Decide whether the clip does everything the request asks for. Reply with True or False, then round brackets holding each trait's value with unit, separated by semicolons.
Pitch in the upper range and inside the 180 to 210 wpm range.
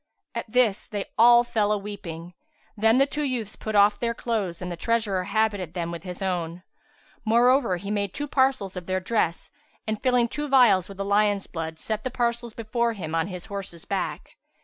True (205 Hz; 195 wpm)